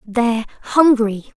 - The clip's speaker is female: Yes, female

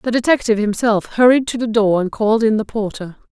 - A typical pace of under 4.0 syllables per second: No, 6.0 syllables/s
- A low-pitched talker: No, high, 220 Hz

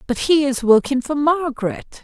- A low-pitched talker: No, very high, 280 Hz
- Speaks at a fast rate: No, average, 175 wpm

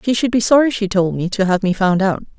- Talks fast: Yes, fast, 300 wpm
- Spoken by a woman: Yes, female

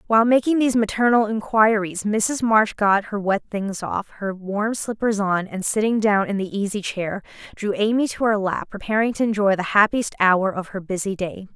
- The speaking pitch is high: Yes, high, 210 Hz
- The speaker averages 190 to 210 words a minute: Yes, average, 195 wpm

